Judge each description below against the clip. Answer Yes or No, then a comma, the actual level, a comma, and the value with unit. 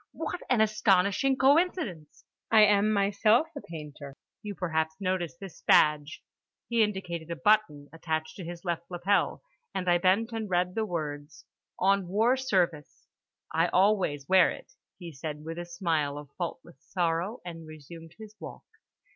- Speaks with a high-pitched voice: No, medium, 180 Hz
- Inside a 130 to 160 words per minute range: Yes, average, 150 wpm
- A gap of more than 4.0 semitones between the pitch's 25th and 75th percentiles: Yes, average, 4.6 semitones